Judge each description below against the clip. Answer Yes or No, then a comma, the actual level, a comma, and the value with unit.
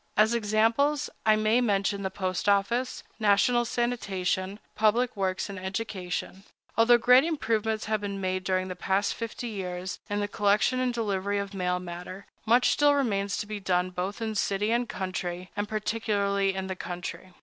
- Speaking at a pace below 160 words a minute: No, average, 170 wpm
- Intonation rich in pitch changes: No, average, 3.2 semitones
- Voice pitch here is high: Yes, high, 205 Hz